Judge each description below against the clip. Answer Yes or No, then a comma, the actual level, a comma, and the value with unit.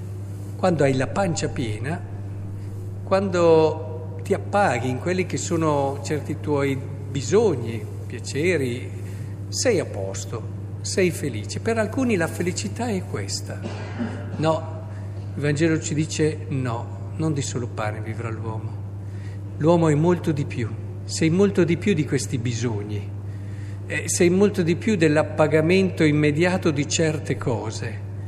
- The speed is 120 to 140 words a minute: Yes, average, 125 wpm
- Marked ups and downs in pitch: Yes, wide, 6.9 semitones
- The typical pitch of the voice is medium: No, low, 110 Hz